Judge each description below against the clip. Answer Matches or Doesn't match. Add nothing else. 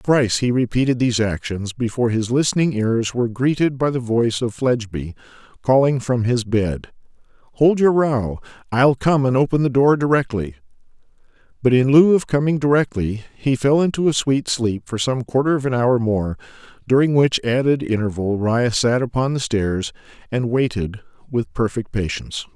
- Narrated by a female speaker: Doesn't match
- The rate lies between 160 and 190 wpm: Matches